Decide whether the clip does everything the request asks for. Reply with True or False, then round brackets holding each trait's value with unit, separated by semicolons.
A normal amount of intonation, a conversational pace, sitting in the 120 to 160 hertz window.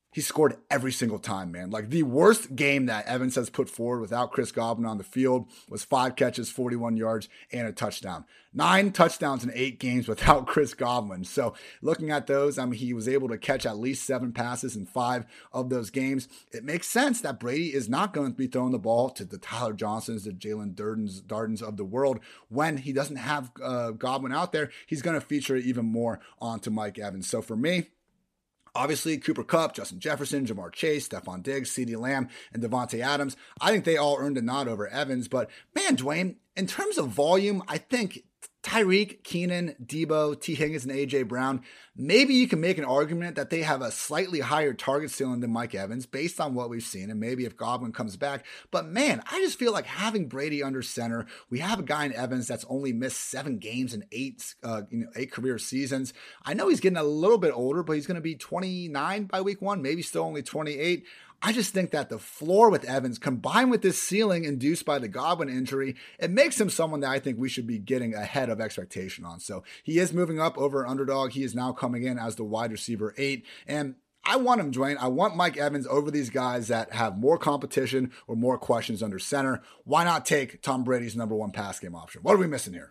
False (4.5 semitones; 220 wpm; 135 Hz)